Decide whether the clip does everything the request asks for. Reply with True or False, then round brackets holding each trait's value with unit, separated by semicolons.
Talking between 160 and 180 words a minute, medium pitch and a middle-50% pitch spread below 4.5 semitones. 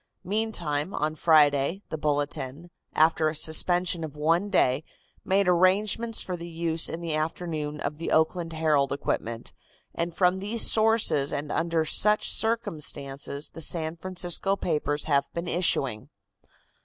False (140 wpm; 165 Hz; 3.4 semitones)